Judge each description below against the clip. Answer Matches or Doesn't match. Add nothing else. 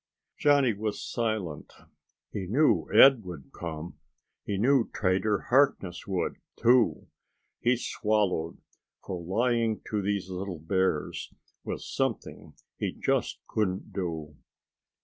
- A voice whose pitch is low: Matches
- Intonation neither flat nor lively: Matches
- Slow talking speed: Matches